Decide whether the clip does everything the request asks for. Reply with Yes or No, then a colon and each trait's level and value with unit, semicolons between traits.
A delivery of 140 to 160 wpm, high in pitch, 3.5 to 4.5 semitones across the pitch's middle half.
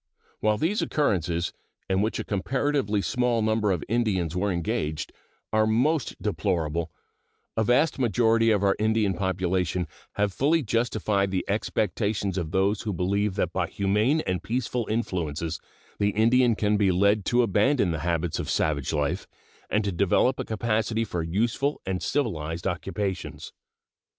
No: average, 150 wpm; low, 100 Hz; average, 3.9 semitones